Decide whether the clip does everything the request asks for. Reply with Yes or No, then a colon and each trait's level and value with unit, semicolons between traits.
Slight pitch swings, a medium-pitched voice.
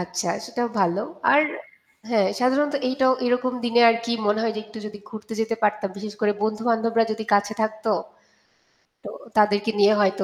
No: narrow, 2.2 semitones; high, 220 Hz